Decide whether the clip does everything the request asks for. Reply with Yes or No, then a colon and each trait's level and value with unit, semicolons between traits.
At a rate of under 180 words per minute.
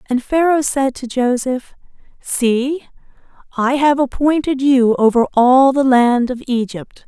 Yes: slow, 135 wpm